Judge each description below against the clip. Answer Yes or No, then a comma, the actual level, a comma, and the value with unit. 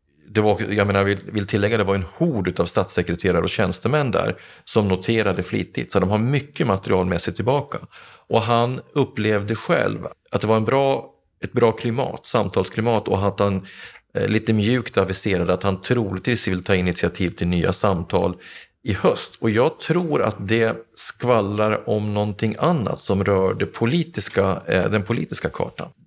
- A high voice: No, low, 105 Hz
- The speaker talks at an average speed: Yes, average, 165 wpm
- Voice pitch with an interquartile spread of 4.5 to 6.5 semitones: No, average, 3.2 semitones